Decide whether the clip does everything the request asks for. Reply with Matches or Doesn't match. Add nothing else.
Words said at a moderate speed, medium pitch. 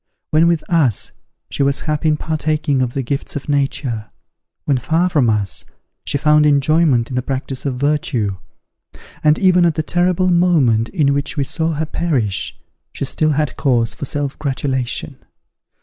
Matches